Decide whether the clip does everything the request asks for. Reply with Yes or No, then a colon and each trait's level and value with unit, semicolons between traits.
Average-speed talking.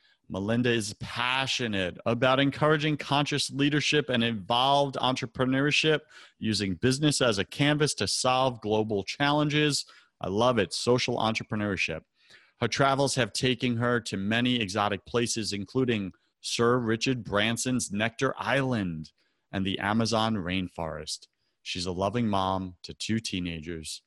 No: slow, 125 wpm